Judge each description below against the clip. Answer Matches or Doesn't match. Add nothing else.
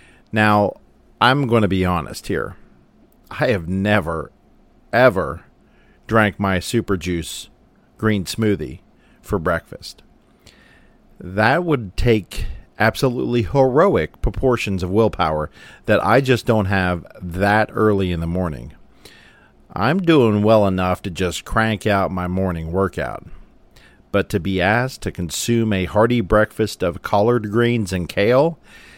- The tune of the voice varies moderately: Matches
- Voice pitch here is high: Doesn't match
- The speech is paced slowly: Matches